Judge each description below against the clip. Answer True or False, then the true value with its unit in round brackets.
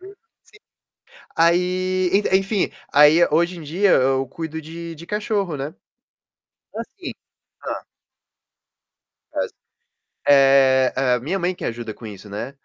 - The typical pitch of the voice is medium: True (160 Hz)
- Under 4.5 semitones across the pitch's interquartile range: False (5.4 semitones)